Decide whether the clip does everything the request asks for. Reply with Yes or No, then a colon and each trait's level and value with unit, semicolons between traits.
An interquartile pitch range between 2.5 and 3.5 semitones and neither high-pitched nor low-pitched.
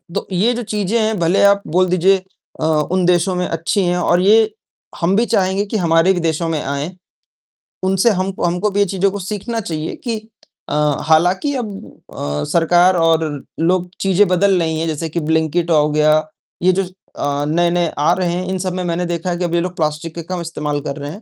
Yes: average, 2.9 semitones; medium, 175 Hz